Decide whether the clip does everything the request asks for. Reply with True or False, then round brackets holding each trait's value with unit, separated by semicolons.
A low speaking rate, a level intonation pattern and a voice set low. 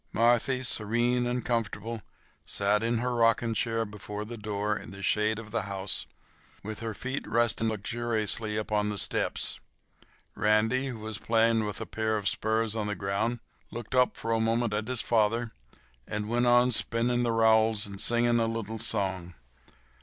False (170 wpm; 1.9 semitones; 110 Hz)